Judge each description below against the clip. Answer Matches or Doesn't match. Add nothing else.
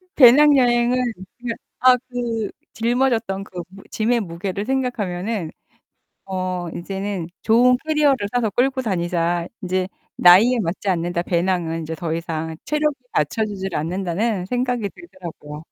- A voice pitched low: Doesn't match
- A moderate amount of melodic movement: Doesn't match